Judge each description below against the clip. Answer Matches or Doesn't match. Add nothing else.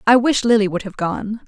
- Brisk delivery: Matches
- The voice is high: Matches